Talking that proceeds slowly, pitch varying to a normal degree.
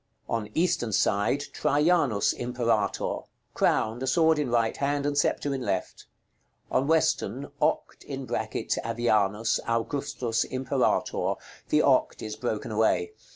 Yes: slow, 110 wpm; average, 4.2 semitones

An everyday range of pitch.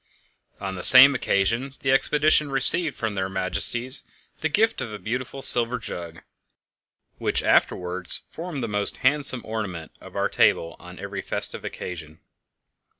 No: wide, 6.3 semitones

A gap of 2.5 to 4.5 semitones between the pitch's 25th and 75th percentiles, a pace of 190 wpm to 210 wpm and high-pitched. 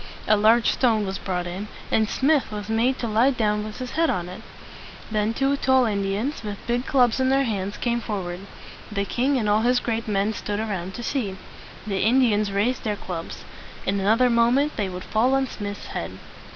Yes: average, 3.6 semitones; average, 200 wpm; high, 220 Hz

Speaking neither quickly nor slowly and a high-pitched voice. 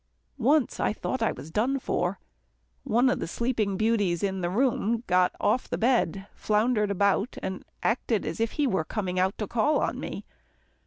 Yes: average, 180 wpm; high, 215 Hz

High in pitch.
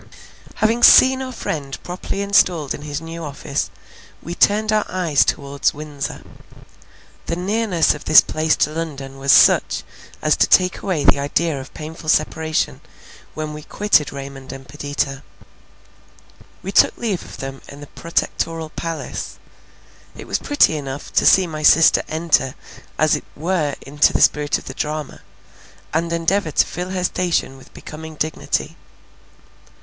No: medium, 155 Hz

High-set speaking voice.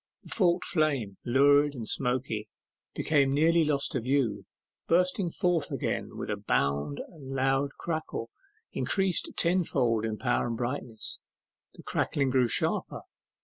No: low, 135 Hz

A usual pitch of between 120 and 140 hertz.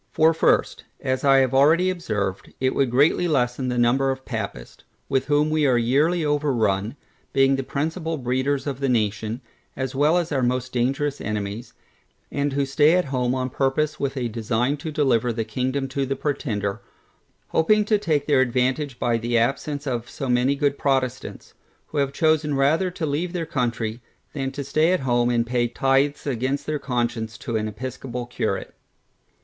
Yes: low, 135 Hz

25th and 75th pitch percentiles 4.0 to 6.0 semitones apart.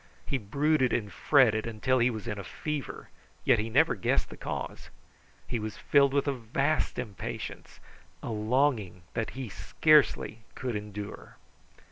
Yes: average, 4.6 semitones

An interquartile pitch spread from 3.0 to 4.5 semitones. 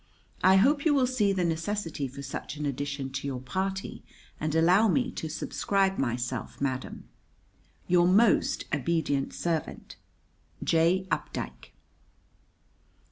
No: wide, 5.5 semitones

